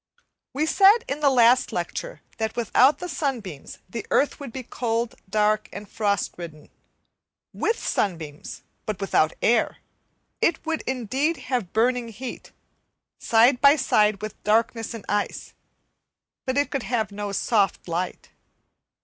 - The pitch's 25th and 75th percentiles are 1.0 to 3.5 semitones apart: No, average, 4.3 semitones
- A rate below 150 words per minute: Yes, average, 140 wpm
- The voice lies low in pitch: No, high, 230 Hz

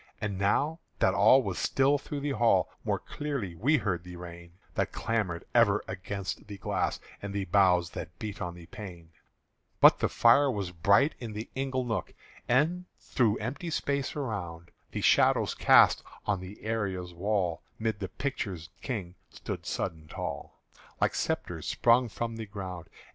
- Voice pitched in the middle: No, low, 105 Hz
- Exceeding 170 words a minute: No, average, 165 wpm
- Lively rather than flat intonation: Yes, wide, 5.7 semitones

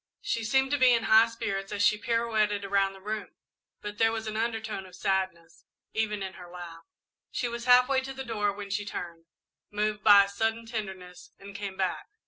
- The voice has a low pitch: No, high, 210 Hz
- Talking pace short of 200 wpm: No, fast, 205 wpm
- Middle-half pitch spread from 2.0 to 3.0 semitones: Yes, average, 2.7 semitones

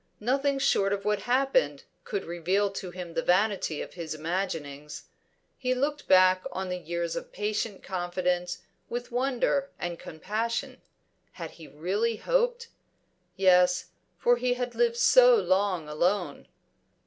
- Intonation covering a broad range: Yes, wide, 6.1 semitones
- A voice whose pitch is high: Yes, high, 200 Hz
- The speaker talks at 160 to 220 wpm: No, average, 140 wpm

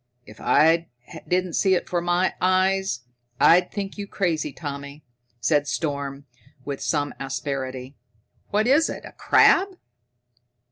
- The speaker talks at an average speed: No, slow, 130 wpm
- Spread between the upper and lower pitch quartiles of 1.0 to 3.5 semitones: No, average, 4.9 semitones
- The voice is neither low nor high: Yes, medium, 165 Hz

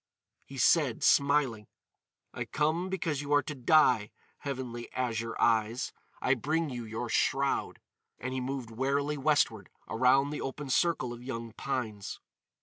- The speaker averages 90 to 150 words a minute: Yes, average, 145 wpm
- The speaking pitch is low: Yes, low, 130 Hz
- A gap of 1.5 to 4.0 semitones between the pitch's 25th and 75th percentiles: Yes, average, 3.7 semitones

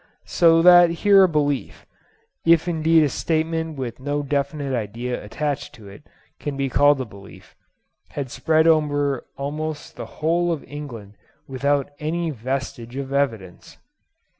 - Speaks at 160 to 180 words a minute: No, slow, 135 wpm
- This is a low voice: No, medium, 145 Hz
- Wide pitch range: No, average, 3.4 semitones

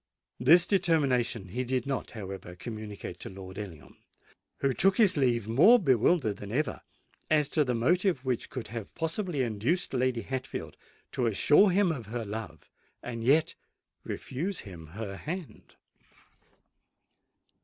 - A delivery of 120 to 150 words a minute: Yes, average, 140 wpm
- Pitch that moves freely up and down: Yes, wide, 6.6 semitones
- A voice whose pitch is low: Yes, low, 125 Hz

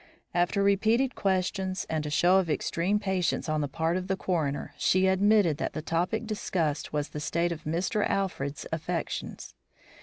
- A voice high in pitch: No, medium, 180 Hz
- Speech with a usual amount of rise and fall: Yes, average, 3.4 semitones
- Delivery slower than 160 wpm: No, average, 170 wpm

